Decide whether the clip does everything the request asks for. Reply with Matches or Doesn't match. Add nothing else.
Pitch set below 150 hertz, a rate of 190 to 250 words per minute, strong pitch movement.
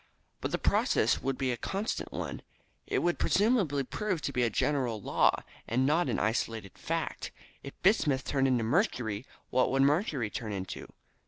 Doesn't match